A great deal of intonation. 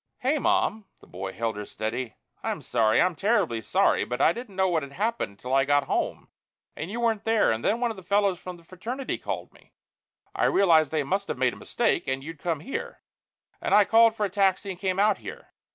Yes: wide, 7.9 semitones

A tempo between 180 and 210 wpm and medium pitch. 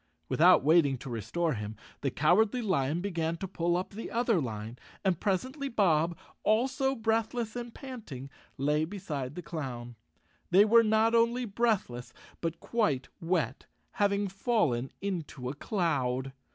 No: average, 145 wpm; medium, 175 Hz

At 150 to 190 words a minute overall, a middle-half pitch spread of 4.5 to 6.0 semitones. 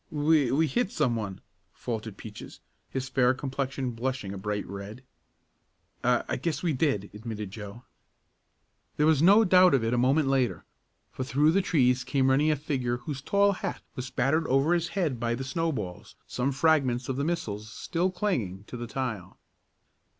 Yes: average, 175 wpm; average, 4.8 semitones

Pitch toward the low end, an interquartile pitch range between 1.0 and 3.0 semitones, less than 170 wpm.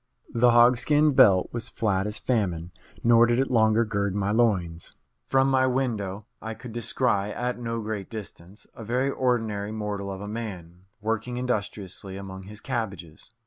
No: low, 110 Hz; average, 3.4 semitones; average, 160 wpm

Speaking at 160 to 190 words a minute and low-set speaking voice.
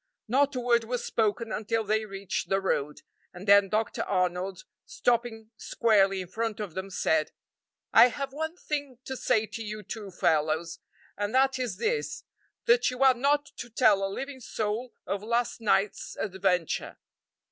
No: average, 165 wpm; high, 220 Hz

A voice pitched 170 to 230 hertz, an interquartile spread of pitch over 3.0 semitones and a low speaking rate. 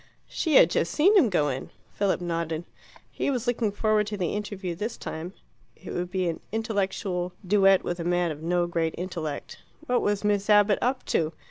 No: high, 190 Hz; average, 3.5 semitones; average, 195 wpm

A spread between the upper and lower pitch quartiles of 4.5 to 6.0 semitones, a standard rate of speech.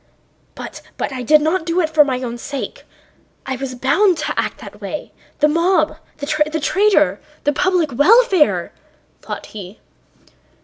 Yes: average, 5.0 semitones; average, 145 wpm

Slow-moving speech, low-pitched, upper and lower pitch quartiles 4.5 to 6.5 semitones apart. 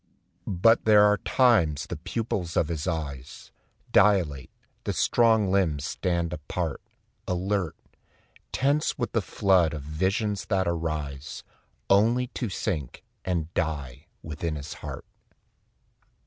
Yes: slow, 120 wpm; very low, 90 Hz; average, 5.2 semitones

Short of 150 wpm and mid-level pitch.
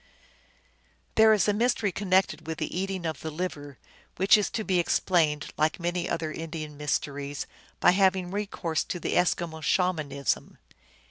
No: average, 155 wpm; medium, 175 Hz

